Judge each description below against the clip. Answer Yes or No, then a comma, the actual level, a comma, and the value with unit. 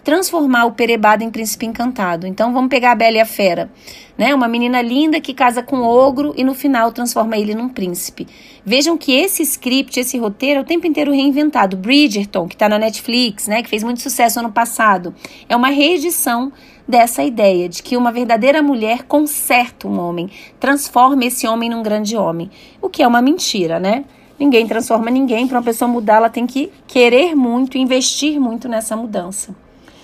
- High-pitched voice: Yes, high, 240 Hz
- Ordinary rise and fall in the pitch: Yes, average, 3.6 semitones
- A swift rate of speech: Yes, fast, 190 wpm